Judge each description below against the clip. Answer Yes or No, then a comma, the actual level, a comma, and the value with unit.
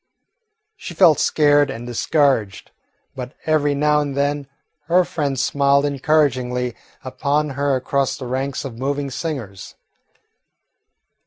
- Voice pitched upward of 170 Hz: No, medium, 140 Hz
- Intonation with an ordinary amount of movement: No, narrow, 2.2 semitones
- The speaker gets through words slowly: Yes, slow, 115 wpm